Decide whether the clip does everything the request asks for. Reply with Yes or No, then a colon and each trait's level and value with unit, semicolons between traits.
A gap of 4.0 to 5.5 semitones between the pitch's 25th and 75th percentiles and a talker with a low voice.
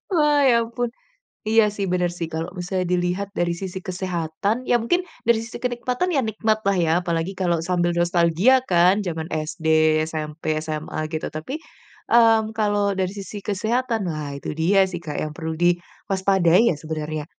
No: average, 4.8 semitones; medium, 185 Hz